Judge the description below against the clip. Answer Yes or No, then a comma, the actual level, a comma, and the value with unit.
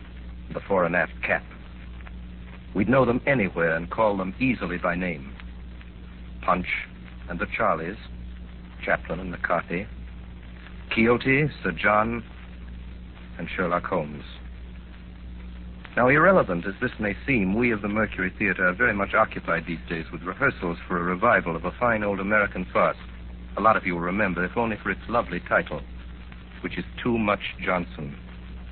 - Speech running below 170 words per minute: Yes, average, 155 wpm